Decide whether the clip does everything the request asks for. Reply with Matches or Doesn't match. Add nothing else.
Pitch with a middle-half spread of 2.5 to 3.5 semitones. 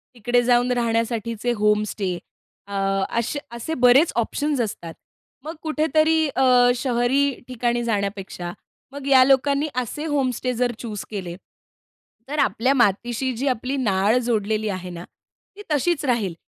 Doesn't match